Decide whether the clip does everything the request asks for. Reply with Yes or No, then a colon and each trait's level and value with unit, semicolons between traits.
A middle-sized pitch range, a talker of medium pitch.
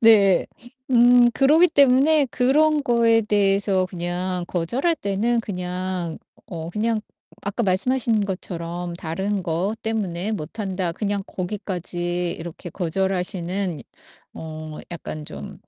No: average, 4.5 semitones; high, 195 Hz